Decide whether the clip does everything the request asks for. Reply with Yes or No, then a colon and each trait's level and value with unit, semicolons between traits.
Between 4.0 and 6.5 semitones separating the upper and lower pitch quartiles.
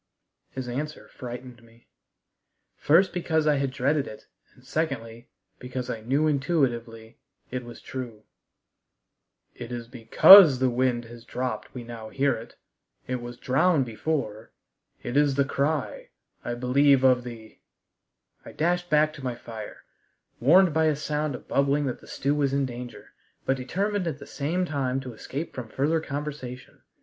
No: average, 3.6 semitones